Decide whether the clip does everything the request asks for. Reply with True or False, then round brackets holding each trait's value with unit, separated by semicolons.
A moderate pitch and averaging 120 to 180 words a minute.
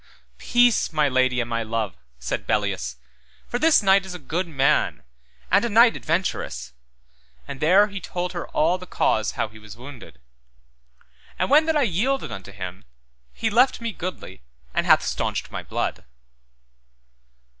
True (170 Hz; 165 wpm)